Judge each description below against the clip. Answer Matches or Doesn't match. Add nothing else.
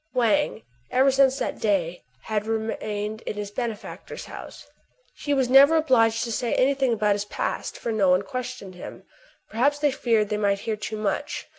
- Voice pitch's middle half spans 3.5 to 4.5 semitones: Matches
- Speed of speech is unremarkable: Matches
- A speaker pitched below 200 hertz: Doesn't match